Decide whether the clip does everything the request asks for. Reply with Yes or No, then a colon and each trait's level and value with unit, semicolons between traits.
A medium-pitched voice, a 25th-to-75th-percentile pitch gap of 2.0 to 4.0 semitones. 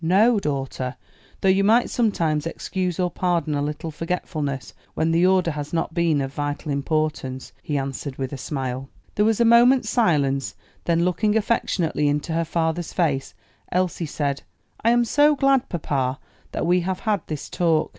No: medium, 165 Hz; average, 4.7 semitones